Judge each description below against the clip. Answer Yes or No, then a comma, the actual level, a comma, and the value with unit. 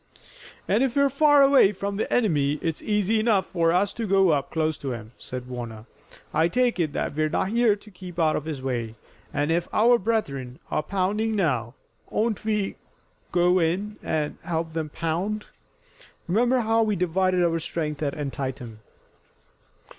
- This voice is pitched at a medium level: Yes, medium, 175 Hz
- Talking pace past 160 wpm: Yes, average, 175 wpm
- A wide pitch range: Yes, wide, 5.9 semitones